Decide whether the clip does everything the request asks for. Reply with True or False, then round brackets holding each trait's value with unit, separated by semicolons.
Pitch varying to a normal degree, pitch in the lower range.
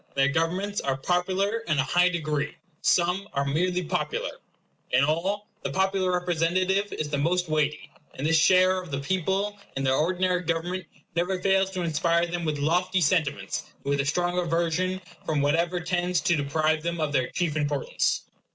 False (3.2 semitones; 170 Hz)